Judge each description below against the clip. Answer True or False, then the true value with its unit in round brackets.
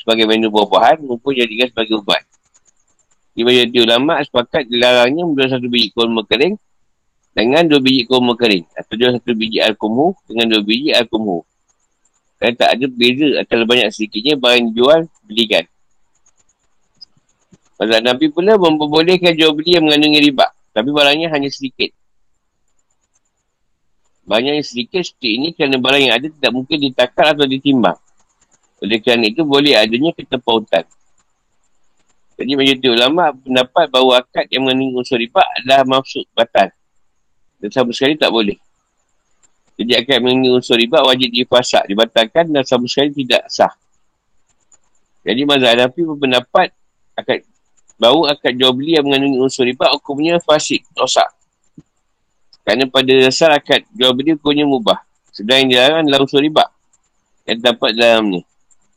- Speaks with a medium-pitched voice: False (130 Hz)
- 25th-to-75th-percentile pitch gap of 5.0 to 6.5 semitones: False (3.5 semitones)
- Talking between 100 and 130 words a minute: False (140 wpm)